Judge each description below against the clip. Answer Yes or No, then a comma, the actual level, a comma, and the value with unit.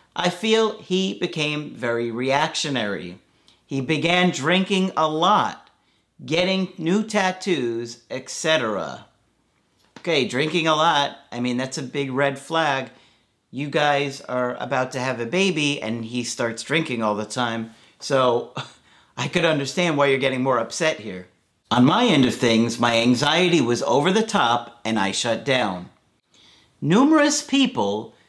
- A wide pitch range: Yes, wide, 6.6 semitones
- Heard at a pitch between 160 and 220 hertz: No, medium, 140 Hz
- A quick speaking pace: No, average, 145 wpm